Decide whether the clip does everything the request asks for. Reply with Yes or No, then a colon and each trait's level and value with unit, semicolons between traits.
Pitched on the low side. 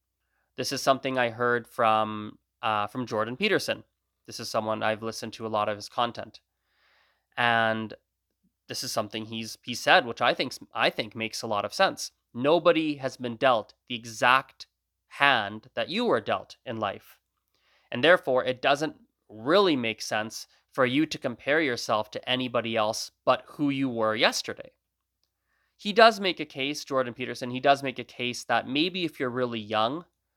Yes: low, 120 Hz